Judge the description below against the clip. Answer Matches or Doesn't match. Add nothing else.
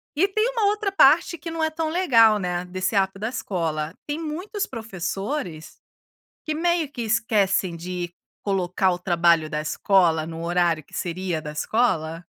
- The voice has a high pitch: Matches